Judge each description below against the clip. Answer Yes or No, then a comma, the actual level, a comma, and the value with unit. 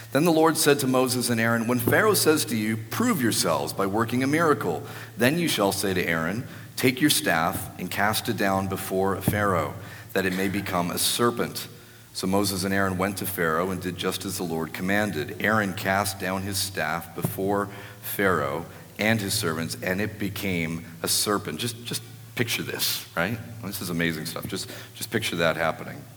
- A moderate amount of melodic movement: Yes, average, 3.9 semitones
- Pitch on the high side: No, low, 100 Hz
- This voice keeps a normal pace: Yes, average, 195 wpm